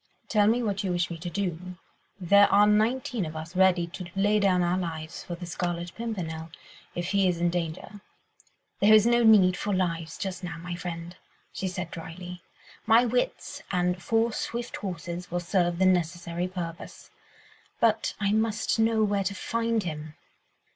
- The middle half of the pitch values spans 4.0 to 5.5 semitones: No, average, 3.2 semitones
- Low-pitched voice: No, medium, 180 Hz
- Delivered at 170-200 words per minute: Yes, average, 175 wpm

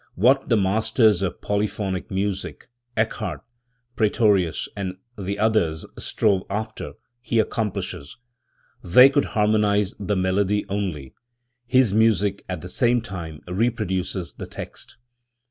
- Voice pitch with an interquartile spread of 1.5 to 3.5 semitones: Yes, average, 2.9 semitones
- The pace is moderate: No, slow, 115 wpm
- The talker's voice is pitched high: No, low, 100 Hz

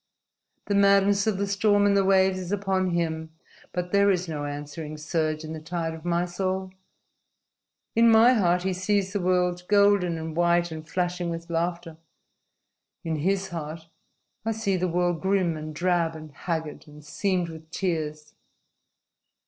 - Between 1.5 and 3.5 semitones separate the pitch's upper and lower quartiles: Yes, average, 3.1 semitones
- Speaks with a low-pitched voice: No, medium, 175 Hz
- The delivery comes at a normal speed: Yes, average, 165 wpm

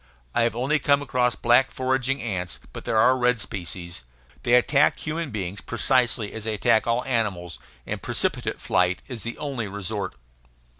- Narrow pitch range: No, average, 4.2 semitones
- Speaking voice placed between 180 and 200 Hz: No, low, 120 Hz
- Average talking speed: Yes, average, 165 wpm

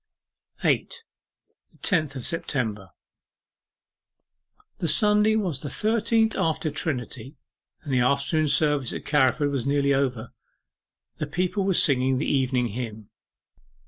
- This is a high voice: No, medium, 145 Hz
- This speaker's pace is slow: Yes, slow, 120 wpm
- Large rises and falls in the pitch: No, average, 4.7 semitones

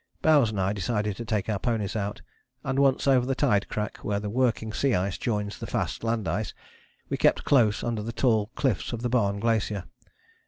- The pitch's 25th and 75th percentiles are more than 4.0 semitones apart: No, average, 3.0 semitones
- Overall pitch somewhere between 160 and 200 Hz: No, low, 110 Hz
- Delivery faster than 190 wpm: Yes, fast, 205 wpm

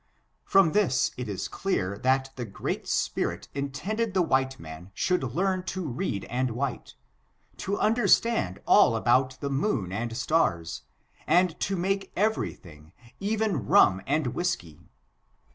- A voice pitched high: No, low, 135 Hz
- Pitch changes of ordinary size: No, wide, 8.8 semitones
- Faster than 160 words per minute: No, average, 140 wpm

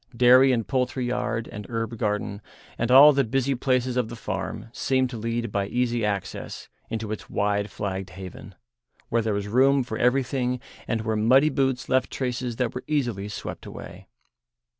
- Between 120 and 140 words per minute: No, average, 175 wpm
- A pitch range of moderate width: Yes, average, 3.4 semitones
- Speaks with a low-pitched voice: Yes, low, 120 Hz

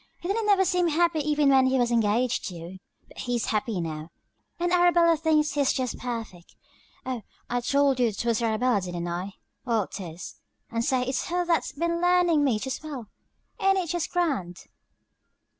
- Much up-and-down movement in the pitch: Yes, wide, 7.4 semitones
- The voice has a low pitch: No, very high, 260 Hz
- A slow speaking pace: No, average, 175 wpm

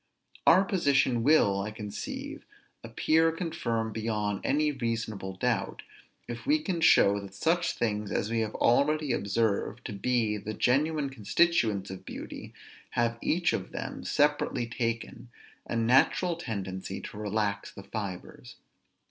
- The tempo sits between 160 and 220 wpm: No, slow, 135 wpm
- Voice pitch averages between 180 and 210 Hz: No, low, 115 Hz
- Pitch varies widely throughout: Yes, wide, 6.0 semitones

